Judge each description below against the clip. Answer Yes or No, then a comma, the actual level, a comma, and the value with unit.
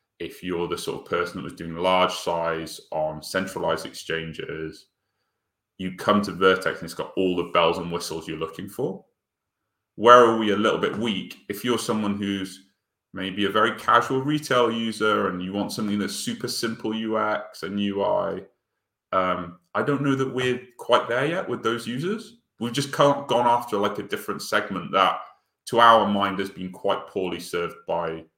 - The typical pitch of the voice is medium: No, low, 100 Hz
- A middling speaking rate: Yes, average, 185 wpm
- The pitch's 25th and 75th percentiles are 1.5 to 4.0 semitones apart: No, average, 4.4 semitones